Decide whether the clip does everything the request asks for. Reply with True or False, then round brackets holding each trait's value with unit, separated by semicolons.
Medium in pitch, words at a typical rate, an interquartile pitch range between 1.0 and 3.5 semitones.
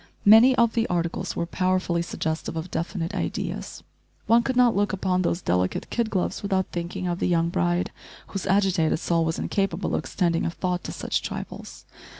True (180 Hz; 180 wpm; 2.9 semitones)